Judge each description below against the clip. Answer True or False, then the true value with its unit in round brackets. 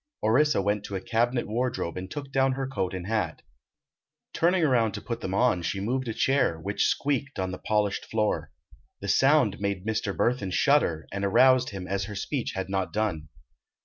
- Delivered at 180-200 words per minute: True (190 wpm)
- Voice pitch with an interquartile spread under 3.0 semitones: False (5.0 semitones)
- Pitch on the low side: True (110 Hz)